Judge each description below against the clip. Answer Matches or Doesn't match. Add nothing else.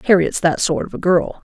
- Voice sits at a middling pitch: Matches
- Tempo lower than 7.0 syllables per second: Matches